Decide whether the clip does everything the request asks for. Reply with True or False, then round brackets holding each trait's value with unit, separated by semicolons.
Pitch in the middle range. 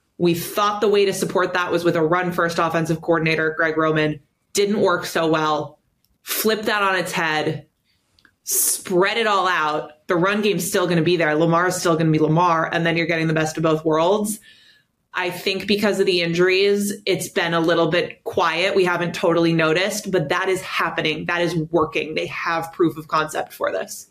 True (175 Hz)